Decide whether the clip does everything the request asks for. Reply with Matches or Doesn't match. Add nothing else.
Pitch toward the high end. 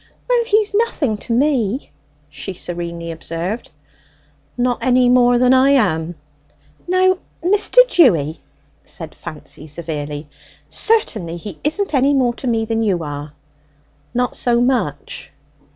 Matches